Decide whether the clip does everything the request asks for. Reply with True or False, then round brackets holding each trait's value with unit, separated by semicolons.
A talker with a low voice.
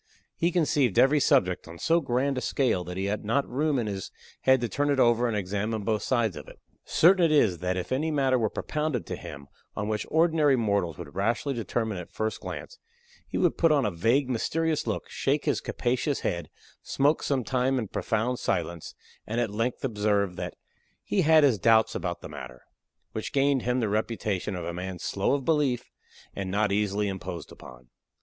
True (115 Hz)